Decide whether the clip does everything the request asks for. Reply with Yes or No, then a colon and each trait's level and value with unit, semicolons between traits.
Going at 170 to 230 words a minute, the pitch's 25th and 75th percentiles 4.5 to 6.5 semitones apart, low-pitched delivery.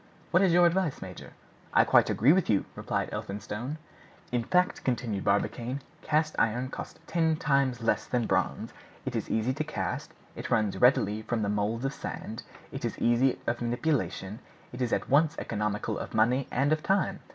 Yes: average, 180 wpm; wide, 5.6 semitones; low, 125 Hz